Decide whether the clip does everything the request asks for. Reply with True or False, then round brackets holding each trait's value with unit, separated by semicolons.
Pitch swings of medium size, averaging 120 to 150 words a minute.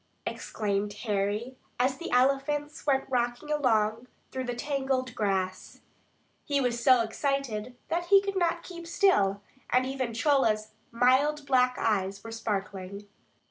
True (4.6 semitones; 135 wpm)